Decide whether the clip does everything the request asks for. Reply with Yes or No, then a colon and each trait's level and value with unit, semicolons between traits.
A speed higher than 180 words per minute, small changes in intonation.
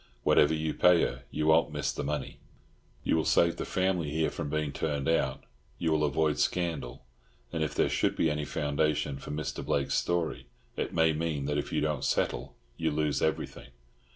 Yes: average, 190 wpm; narrow, 1.8 semitones